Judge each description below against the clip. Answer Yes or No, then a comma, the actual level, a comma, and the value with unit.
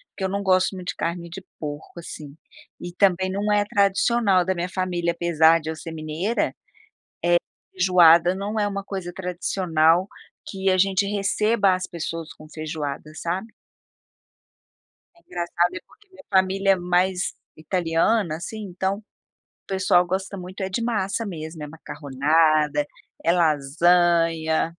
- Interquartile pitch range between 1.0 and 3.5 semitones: Yes, average, 2.9 semitones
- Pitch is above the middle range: No, medium, 180 Hz